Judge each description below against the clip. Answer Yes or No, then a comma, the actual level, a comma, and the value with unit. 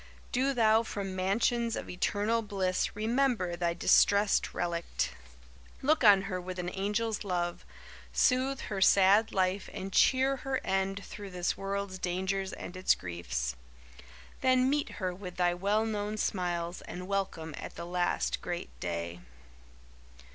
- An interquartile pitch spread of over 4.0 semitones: No, average, 3.4 semitones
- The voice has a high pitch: Yes, high, 195 Hz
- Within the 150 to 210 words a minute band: No, average, 140 wpm